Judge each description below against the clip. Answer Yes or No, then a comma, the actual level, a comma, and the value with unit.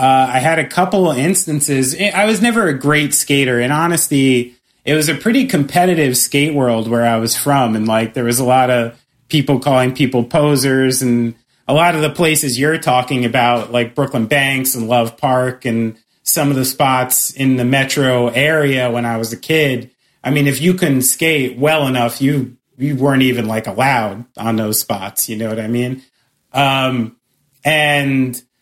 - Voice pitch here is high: No, low, 130 Hz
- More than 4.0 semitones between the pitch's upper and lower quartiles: No, average, 3.3 semitones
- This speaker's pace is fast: No, average, 185 wpm